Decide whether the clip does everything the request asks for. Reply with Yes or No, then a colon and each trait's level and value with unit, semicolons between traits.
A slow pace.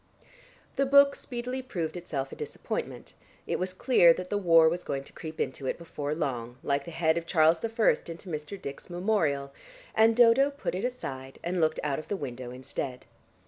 No: average, 190 wpm